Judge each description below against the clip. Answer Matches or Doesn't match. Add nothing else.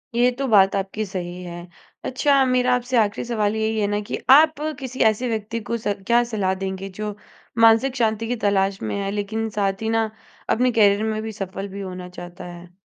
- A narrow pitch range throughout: Doesn't match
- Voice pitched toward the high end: Matches